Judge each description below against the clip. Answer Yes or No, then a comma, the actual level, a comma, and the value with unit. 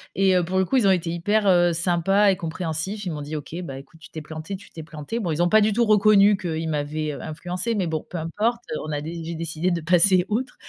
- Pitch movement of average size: Yes, average, 3.8 semitones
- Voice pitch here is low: No, medium, 175 Hz